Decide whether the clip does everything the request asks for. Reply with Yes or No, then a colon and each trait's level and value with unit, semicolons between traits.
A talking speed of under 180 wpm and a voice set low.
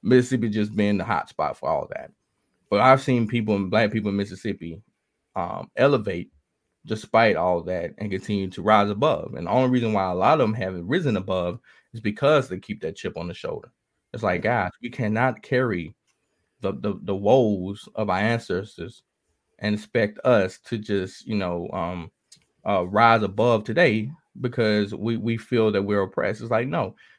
No: average, 185 wpm; low, 105 Hz